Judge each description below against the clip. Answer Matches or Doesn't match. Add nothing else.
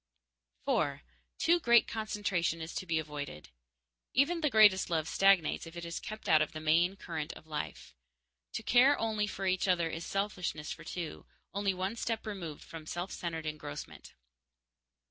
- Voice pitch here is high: Doesn't match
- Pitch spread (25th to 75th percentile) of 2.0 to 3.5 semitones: Doesn't match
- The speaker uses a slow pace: Doesn't match